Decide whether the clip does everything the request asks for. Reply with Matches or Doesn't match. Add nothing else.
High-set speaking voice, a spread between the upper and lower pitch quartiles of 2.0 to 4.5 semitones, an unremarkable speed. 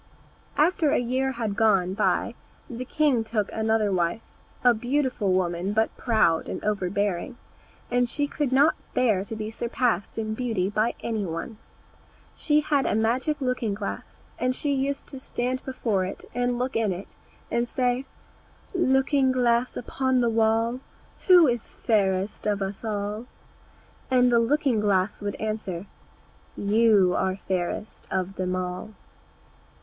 Matches